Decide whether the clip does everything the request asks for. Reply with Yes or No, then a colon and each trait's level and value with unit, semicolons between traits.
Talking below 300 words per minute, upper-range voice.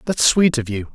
No: fast, 255 wpm; low, 135 Hz